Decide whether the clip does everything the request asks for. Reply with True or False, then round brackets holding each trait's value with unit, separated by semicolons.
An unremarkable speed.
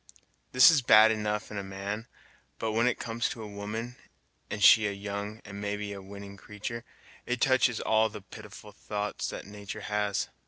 True (185 wpm)